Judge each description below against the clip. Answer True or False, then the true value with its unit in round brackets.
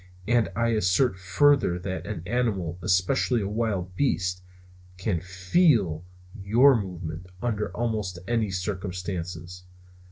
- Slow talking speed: True (115 wpm)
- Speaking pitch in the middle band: False (95 Hz)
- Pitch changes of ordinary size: True (4.1 semitones)